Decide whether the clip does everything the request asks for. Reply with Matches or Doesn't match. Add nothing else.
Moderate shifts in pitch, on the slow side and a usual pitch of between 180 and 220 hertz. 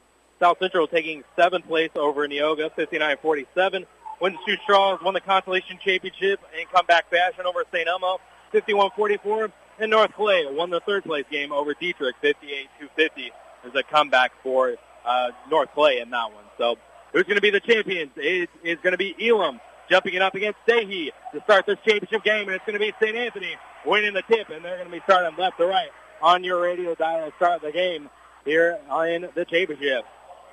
Doesn't match